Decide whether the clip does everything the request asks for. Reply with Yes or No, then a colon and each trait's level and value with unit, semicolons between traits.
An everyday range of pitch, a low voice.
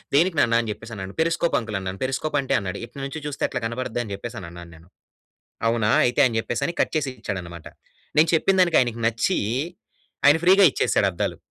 No: wide, 6.2 semitones; low, 120 Hz